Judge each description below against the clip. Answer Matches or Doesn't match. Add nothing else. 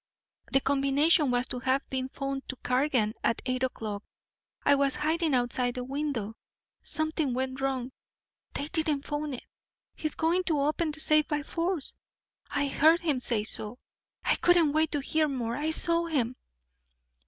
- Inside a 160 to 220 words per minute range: Matches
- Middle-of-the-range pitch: Doesn't match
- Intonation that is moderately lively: Matches